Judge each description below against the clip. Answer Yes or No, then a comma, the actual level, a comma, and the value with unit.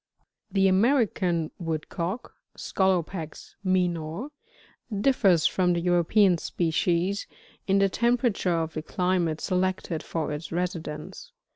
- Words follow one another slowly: Yes, slow, 120 wpm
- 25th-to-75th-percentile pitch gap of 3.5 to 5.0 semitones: No, average, 3.0 semitones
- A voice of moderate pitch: Yes, medium, 180 Hz